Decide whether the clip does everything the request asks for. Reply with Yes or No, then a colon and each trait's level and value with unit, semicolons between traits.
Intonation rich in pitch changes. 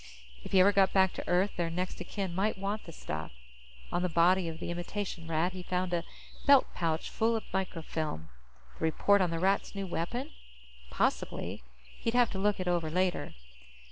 No: average, 2.8 semitones